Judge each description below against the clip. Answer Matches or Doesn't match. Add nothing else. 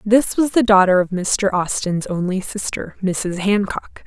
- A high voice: Matches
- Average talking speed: Matches